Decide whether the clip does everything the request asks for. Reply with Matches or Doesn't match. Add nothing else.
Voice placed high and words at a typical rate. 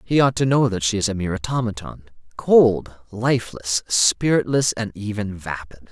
Doesn't match